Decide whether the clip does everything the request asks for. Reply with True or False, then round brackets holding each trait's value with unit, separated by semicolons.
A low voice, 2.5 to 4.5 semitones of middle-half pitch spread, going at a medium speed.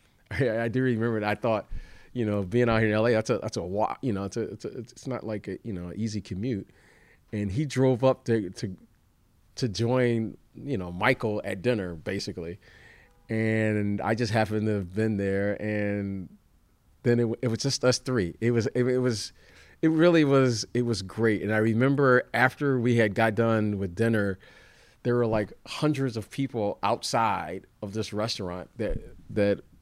True (110 Hz; 3.2 semitones; 190 wpm)